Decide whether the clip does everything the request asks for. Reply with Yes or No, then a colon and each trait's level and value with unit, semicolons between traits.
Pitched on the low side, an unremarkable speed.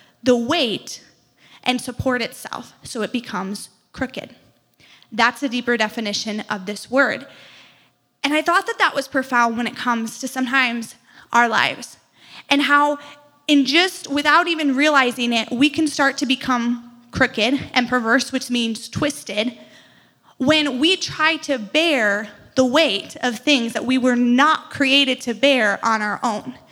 No: very high, 255 Hz; average, 155 wpm